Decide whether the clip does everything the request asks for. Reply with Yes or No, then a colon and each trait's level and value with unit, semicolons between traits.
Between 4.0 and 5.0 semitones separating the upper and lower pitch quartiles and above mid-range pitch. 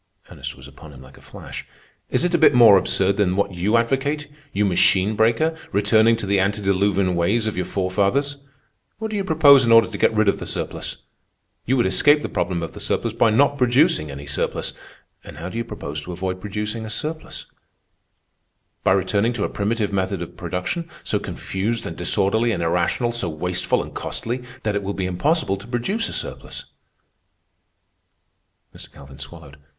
No: average, 4.4 semitones; low, 105 Hz